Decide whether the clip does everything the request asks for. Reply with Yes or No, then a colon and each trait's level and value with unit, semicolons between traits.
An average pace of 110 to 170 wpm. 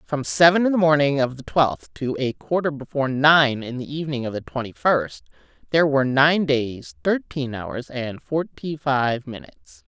No: average, 180 wpm